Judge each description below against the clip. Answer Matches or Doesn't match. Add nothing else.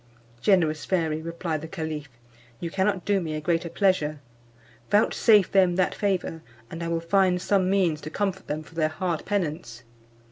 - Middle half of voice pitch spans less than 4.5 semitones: Matches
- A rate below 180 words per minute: Matches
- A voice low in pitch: Doesn't match